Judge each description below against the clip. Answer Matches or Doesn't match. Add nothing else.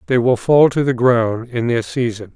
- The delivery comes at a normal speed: Doesn't match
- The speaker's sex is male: Matches